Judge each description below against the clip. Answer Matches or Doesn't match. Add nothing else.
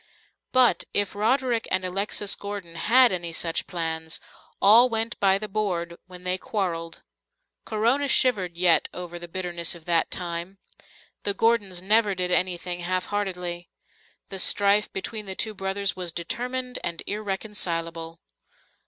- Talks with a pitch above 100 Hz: Matches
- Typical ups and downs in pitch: Matches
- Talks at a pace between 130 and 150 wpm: Matches